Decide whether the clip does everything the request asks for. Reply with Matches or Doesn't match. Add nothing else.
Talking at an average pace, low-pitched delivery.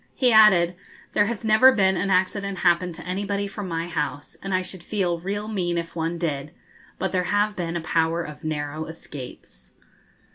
Doesn't match